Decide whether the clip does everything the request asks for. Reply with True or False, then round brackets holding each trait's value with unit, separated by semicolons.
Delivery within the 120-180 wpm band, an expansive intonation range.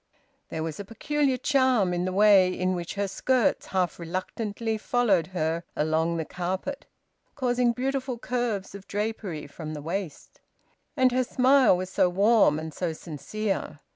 True (155 wpm; 5.9 semitones)